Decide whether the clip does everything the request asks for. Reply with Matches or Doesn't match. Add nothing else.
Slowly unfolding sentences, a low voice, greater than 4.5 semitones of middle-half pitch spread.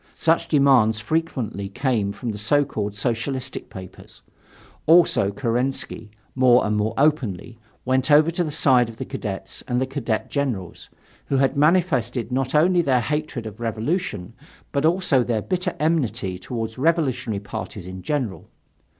Doesn't match